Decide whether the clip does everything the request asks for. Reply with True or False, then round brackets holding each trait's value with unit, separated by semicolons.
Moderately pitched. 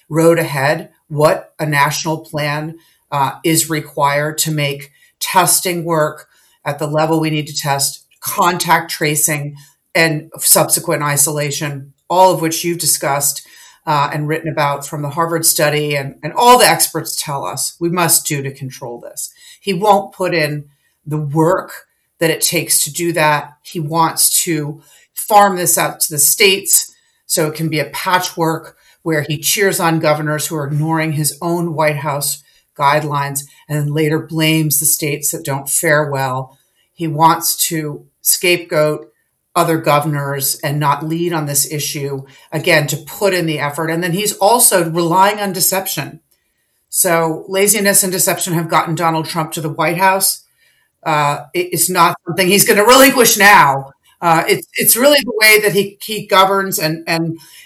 True (160 Hz)